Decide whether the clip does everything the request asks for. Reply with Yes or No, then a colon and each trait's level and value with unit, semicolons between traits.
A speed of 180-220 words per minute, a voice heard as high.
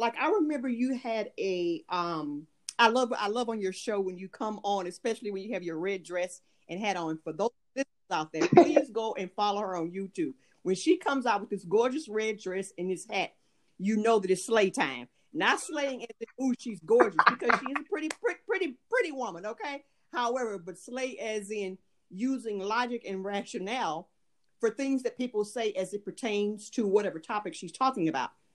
Yes: average, 200 wpm; high, 220 Hz